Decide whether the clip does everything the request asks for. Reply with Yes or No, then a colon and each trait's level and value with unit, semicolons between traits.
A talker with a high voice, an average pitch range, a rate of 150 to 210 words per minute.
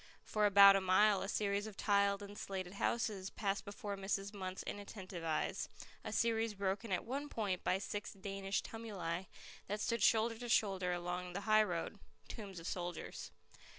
No: high, 200 Hz; narrow, 2.2 semitones; average, 165 wpm